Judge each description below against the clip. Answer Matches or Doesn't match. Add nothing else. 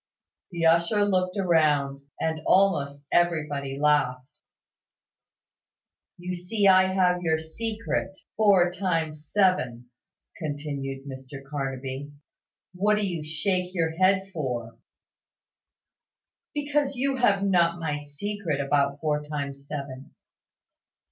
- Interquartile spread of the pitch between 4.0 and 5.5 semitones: Matches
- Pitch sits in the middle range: Matches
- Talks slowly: Matches